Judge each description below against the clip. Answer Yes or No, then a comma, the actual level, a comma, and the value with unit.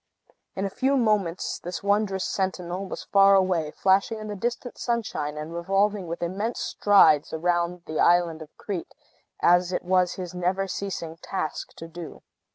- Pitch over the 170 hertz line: Yes, medium, 185 Hz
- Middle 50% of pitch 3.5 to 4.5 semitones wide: No, average, 2.7 semitones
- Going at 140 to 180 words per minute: Yes, average, 165 wpm